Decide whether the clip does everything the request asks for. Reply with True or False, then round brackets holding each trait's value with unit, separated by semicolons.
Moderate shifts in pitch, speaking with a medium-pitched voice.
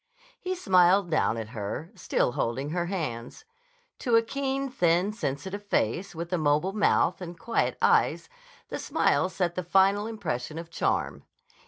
True (4.9 semitones; 180 Hz)